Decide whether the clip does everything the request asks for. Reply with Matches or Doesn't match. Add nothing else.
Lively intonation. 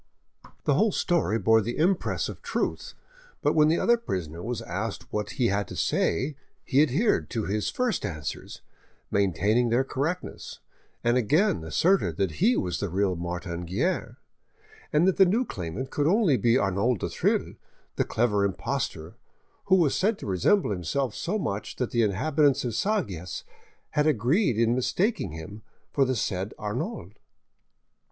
Matches